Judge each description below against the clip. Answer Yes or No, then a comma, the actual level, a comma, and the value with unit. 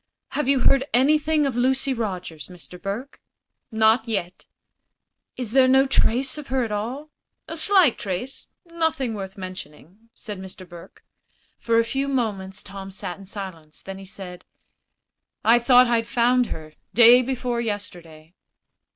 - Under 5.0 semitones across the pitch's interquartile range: No, wide, 5.5 semitones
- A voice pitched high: Yes, high, 230 Hz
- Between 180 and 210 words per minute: No, average, 150 wpm